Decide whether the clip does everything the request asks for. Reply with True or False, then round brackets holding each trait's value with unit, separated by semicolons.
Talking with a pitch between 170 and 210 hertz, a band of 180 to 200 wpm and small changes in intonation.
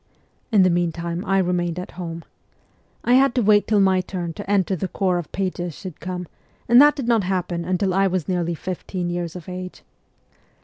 True (185 Hz; 195 wpm; 2.0 semitones)